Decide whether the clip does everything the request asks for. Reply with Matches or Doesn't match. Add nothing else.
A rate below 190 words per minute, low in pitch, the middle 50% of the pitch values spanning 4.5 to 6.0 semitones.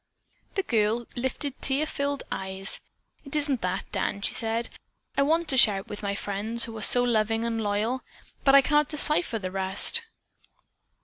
Doesn't match